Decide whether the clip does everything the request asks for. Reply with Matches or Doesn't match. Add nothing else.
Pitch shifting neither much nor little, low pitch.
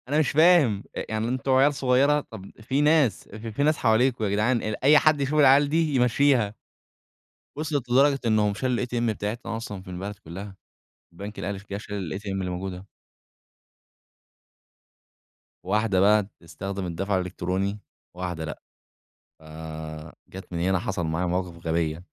Doesn't match